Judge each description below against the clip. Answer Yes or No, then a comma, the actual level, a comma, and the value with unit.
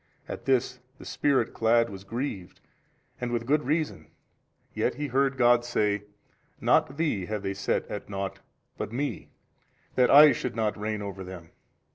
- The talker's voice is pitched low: Yes, low, 115 Hz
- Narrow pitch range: No, average, 4.7 semitones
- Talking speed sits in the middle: Yes, average, 160 wpm